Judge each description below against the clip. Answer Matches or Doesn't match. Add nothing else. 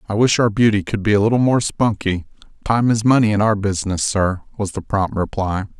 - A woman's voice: Doesn't match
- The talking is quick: Matches